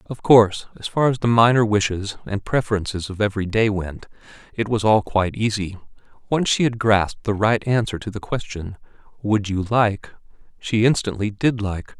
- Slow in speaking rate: No, average, 180 wpm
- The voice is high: No, low, 105 Hz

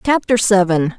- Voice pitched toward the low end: No, high, 205 Hz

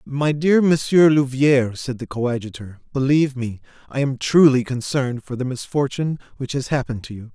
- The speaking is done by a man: Yes, male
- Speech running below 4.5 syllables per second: No, 5.6 syllables/s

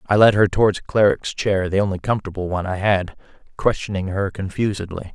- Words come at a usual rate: Yes, average, 175 wpm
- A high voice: No, low, 100 Hz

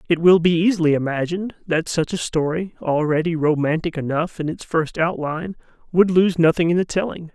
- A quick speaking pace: No, average, 180 wpm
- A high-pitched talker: No, medium, 165 Hz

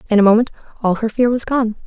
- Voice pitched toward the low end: No, high, 225 Hz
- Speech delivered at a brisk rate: Yes, fast, 255 wpm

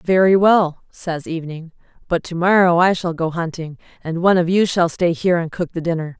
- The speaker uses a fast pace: Yes, fast, 215 wpm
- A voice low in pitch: No, medium, 170 Hz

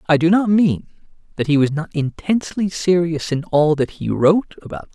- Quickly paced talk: Yes, fast, 220 wpm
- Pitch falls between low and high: Yes, medium, 165 Hz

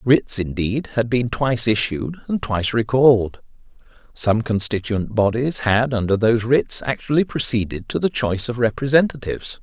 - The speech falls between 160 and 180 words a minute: No, average, 145 wpm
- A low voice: Yes, low, 115 Hz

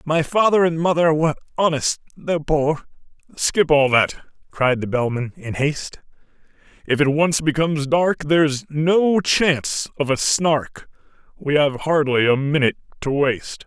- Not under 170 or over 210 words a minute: No, average, 150 wpm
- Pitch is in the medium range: Yes, medium, 150 Hz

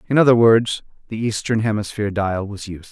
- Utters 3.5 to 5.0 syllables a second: No, 6.4 syllables/s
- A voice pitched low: Yes, low, 110 Hz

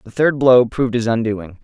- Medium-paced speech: No, fast, 220 wpm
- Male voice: Yes, male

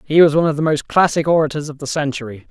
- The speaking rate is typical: No, fast, 265 wpm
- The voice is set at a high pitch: No, medium, 150 Hz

